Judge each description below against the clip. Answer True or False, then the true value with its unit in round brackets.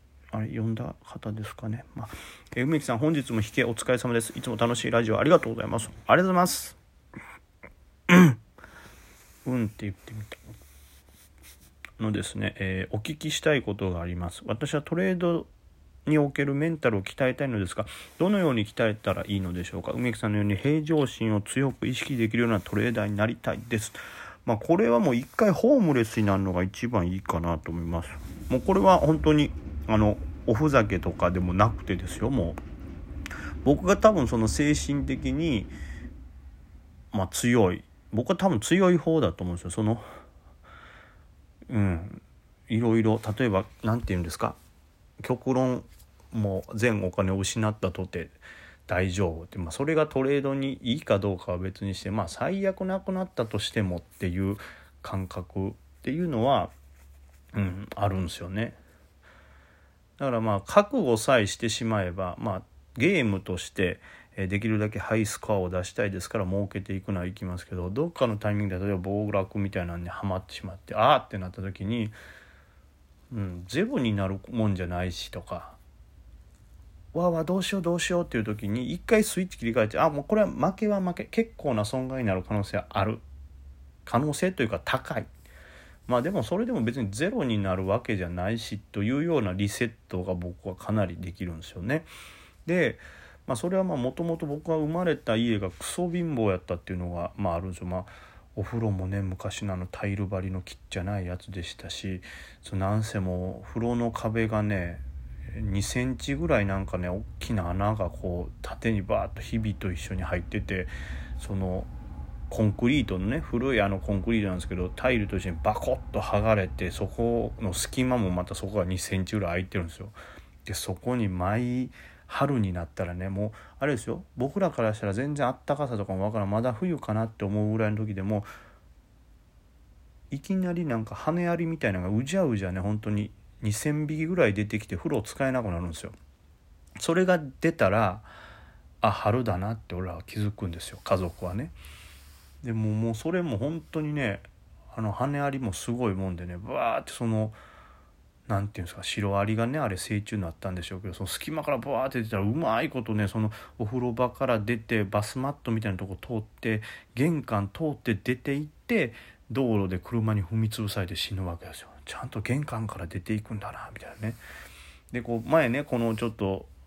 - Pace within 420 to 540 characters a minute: False (370 characters per minute)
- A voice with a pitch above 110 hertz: False (105 Hz)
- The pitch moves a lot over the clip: False (4.9 semitones)